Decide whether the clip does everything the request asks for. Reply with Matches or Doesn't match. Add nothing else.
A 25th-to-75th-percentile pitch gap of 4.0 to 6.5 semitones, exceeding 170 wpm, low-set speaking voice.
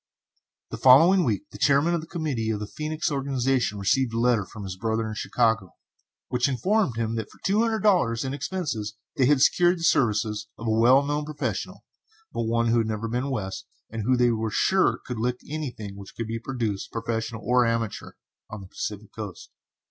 Matches